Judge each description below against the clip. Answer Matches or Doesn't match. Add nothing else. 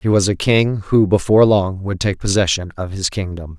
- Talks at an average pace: Doesn't match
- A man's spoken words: Matches